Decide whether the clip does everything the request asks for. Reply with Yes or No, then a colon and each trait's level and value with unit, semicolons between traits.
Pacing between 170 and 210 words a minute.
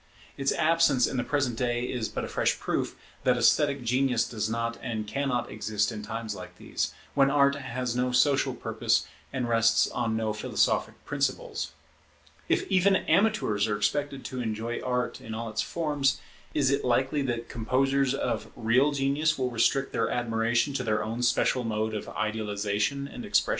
Yes: average, 175 wpm